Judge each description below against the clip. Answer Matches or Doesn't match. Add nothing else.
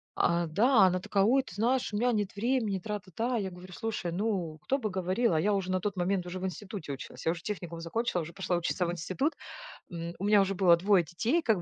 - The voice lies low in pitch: Doesn't match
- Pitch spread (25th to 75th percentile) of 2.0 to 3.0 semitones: Doesn't match